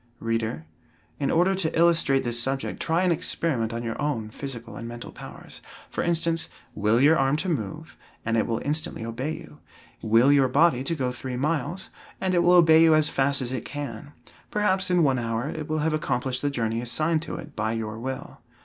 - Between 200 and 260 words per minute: Yes, fast, 205 wpm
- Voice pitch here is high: No, medium, 140 Hz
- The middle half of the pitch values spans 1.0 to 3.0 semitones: No, wide, 5.5 semitones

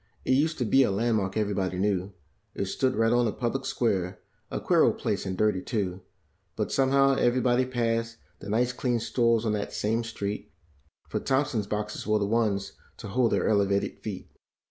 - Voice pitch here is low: Yes, low, 110 Hz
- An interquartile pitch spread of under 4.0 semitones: Yes, average, 3.3 semitones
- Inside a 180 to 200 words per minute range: Yes, average, 190 wpm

